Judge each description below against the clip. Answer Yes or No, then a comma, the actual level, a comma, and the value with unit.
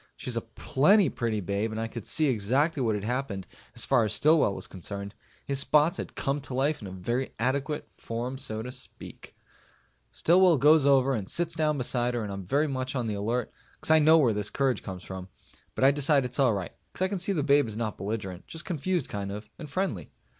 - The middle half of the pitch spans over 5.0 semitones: Yes, wide, 5.4 semitones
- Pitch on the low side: Yes, low, 130 Hz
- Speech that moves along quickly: Yes, fast, 220 wpm